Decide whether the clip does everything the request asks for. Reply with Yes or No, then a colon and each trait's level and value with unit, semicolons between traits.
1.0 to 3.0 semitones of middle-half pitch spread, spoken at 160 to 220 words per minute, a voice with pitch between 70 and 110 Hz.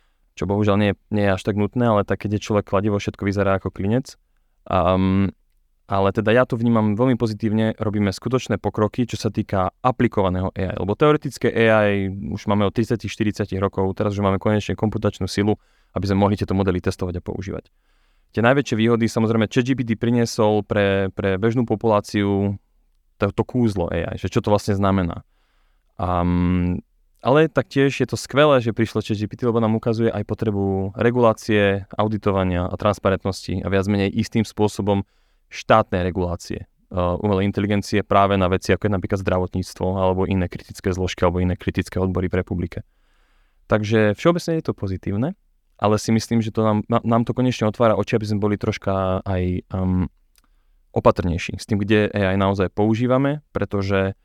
Yes: average, 2.7 semitones; fast, 165 wpm; low, 105 Hz